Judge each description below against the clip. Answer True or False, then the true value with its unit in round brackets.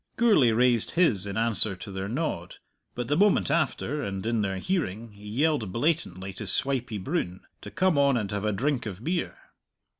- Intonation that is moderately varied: False (6.7 semitones)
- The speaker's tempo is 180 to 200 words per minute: True (185 wpm)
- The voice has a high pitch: False (115 Hz)